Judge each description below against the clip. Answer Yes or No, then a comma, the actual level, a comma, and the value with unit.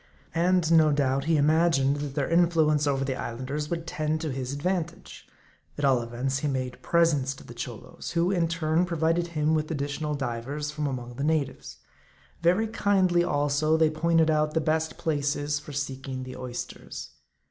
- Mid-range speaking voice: Yes, medium, 150 Hz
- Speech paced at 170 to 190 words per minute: Yes, average, 175 wpm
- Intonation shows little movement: No, average, 3.1 semitones